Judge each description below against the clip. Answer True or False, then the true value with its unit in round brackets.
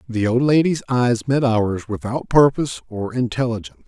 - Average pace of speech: True (155 wpm)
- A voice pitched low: True (120 Hz)